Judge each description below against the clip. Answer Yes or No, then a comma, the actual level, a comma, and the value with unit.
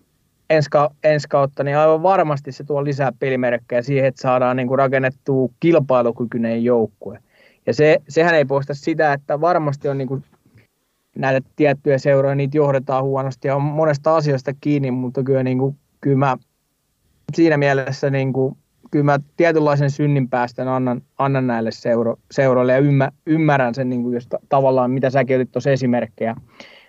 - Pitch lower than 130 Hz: No, low, 135 Hz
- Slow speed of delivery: No, average, 150 wpm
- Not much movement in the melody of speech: Yes, narrow, 2.3 semitones